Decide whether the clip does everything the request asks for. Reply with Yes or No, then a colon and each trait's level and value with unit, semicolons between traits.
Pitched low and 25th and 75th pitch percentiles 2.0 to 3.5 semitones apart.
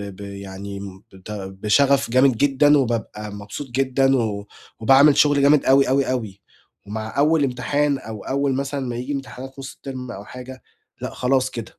No: low, 130 Hz; average, 4.6 semitones